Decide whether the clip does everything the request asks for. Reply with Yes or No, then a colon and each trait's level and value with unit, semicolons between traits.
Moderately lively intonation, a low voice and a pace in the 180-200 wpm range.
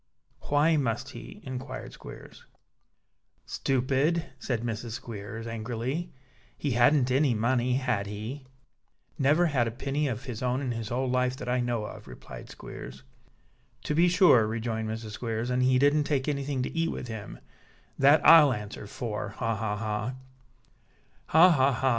No: average, 3.7 semitones; low, 125 Hz; average, 160 wpm